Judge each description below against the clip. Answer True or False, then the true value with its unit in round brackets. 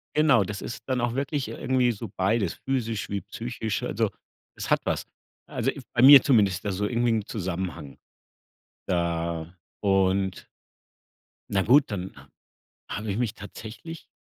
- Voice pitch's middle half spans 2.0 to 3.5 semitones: False (4.2 semitones)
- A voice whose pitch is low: True (105 Hz)